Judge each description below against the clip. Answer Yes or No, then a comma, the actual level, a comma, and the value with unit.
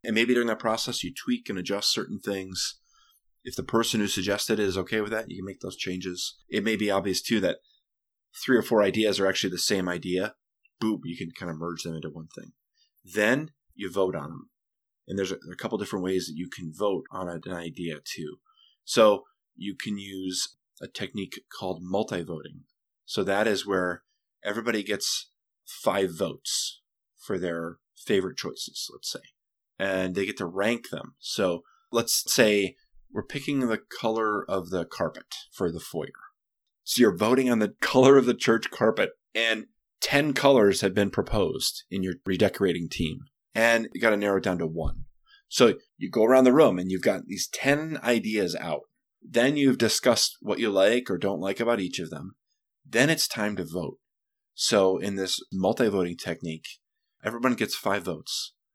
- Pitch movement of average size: Yes, average, 4.3 semitones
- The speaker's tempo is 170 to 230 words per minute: Yes, average, 190 wpm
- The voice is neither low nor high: No, low, 100 Hz